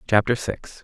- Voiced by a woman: No, male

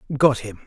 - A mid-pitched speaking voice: No, low, 125 Hz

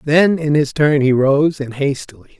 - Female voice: No, male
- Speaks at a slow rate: No, average, 200 wpm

